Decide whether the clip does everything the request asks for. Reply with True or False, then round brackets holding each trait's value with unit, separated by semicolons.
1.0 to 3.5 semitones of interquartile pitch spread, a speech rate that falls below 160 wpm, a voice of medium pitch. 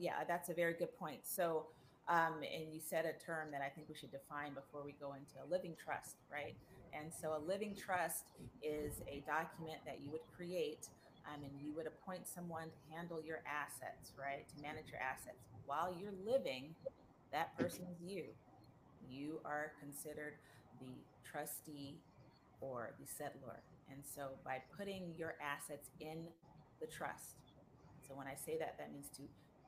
False (2.7 semitones; 175 wpm; 150 Hz)